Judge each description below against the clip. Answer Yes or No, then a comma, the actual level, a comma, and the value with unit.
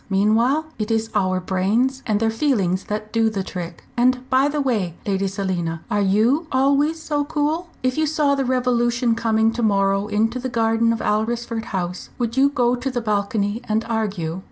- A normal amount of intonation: Yes, average, 4.1 semitones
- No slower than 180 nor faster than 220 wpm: Yes, average, 185 wpm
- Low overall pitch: No, high, 225 Hz